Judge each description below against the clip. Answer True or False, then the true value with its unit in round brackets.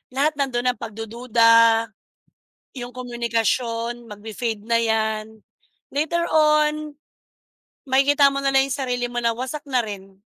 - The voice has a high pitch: True (240 Hz)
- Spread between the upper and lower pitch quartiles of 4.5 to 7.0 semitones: False (3.5 semitones)